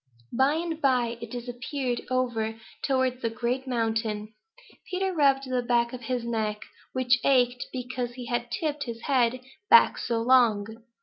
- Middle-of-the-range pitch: No, high, 245 Hz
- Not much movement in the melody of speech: Yes, narrow, 1.9 semitones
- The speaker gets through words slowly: No, average, 150 wpm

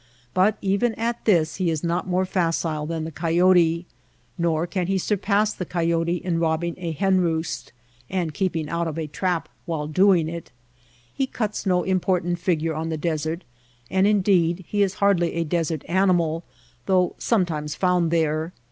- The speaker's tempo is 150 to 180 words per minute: Yes, average, 170 wpm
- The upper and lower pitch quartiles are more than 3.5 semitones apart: No, narrow, 2.5 semitones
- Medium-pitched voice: Yes, medium, 170 Hz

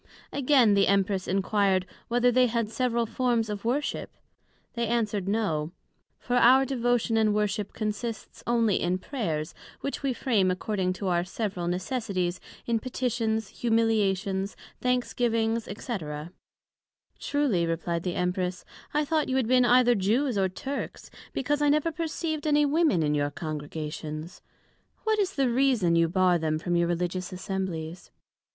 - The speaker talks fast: No, average, 145 wpm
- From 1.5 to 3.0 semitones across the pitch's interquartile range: No, average, 5.3 semitones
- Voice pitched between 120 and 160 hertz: No, high, 215 Hz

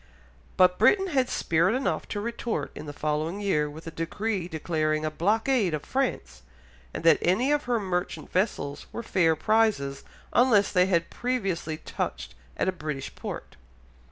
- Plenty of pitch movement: Yes, wide, 6.3 semitones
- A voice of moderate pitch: Yes, medium, 180 Hz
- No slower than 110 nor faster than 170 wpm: Yes, average, 160 wpm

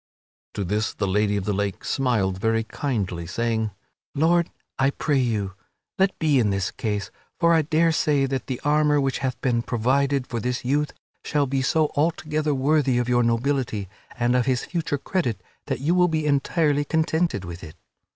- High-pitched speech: No, low, 130 Hz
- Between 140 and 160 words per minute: No, average, 180 wpm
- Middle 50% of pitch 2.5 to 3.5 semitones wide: No, average, 5.1 semitones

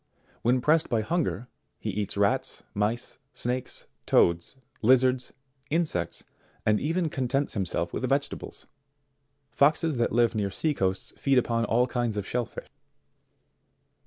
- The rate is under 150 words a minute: Yes, slow, 135 wpm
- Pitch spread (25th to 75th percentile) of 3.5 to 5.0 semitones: Yes, average, 4.3 semitones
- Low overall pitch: Yes, low, 120 Hz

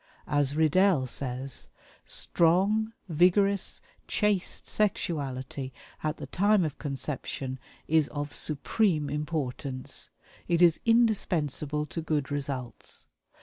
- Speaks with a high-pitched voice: No, medium, 150 Hz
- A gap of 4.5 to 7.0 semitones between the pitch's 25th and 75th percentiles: Yes, average, 4.8 semitones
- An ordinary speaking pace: No, slow, 100 wpm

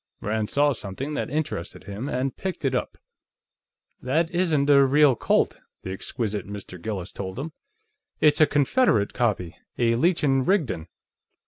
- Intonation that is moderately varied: No, wide, 6.5 semitones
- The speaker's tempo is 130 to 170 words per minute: Yes, average, 150 wpm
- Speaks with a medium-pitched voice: No, low, 130 Hz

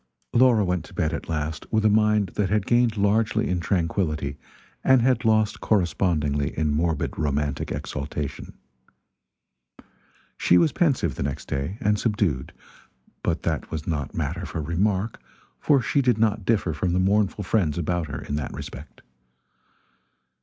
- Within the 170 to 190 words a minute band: No, average, 155 wpm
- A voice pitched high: No, very low, 90 Hz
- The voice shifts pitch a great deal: Yes, wide, 5.7 semitones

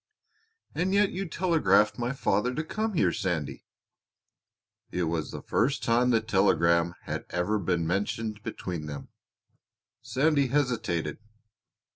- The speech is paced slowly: Yes, slow, 125 wpm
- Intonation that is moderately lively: No, wide, 7.9 semitones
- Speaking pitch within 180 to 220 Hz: No, low, 110 Hz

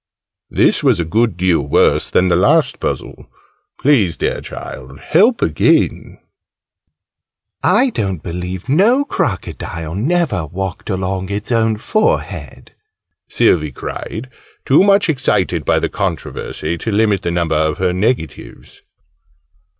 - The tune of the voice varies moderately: No, wide, 7.3 semitones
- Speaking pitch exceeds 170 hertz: No, very low, 95 Hz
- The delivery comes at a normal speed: No, slow, 125 wpm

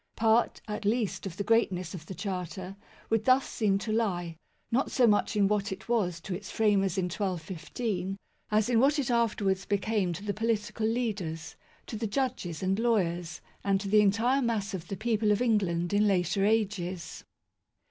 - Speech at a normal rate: Yes, average, 180 wpm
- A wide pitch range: No, average, 3.2 semitones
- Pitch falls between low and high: No, high, 205 Hz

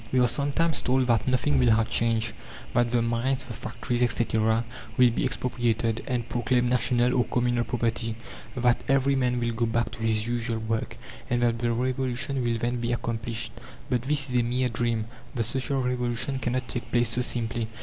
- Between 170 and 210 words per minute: Yes, average, 190 wpm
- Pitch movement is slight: Yes, narrow, 1.4 semitones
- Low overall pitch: Yes, low, 120 Hz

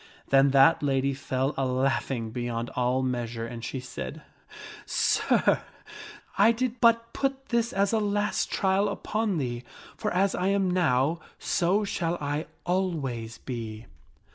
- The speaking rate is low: No, average, 145 wpm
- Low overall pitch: No, medium, 145 Hz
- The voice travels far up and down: Yes, wide, 7.9 semitones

